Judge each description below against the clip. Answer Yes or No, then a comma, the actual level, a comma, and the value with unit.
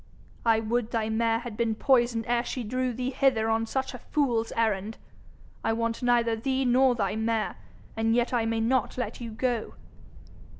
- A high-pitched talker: Yes, high, 230 Hz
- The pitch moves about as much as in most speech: No, narrow, 1.8 semitones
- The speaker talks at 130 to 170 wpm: No, average, 180 wpm